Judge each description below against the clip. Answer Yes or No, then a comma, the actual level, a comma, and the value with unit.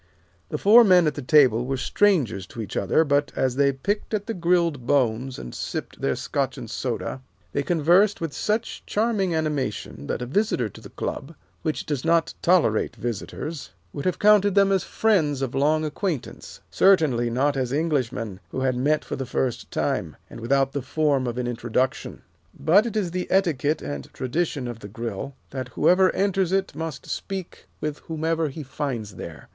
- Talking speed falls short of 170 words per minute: No, average, 185 wpm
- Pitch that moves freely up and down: Yes, wide, 5.9 semitones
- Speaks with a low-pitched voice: No, medium, 145 Hz